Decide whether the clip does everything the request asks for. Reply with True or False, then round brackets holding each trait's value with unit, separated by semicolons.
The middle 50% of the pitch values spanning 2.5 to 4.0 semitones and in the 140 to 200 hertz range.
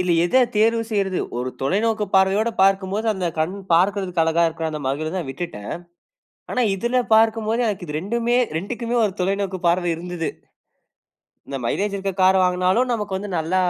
True (3.6 semitones; 190 Hz)